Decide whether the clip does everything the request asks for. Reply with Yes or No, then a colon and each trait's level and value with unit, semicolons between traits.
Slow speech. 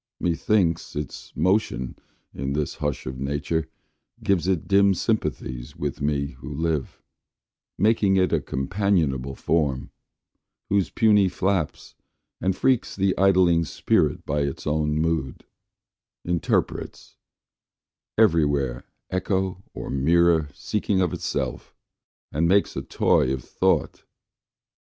Yes: slow, 115 wpm